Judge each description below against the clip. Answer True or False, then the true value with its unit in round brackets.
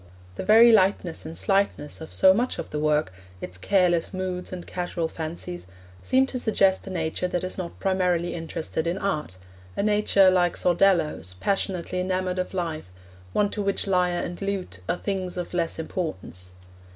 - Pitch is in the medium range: True (180 Hz)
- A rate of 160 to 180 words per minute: True (170 wpm)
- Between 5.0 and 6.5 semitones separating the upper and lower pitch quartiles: False (2.8 semitones)